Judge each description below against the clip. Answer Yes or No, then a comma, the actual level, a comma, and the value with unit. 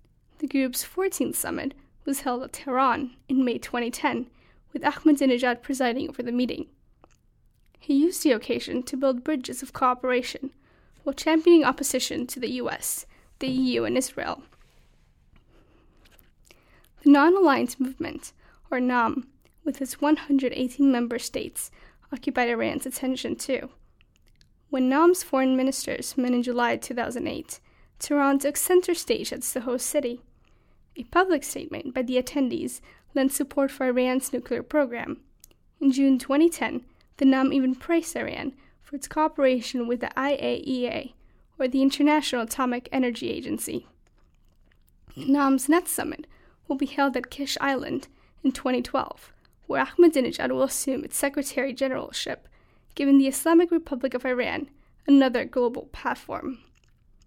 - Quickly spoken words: No, slow, 135 wpm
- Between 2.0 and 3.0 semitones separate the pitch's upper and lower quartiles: Yes, narrow, 2.4 semitones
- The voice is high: Yes, very high, 270 Hz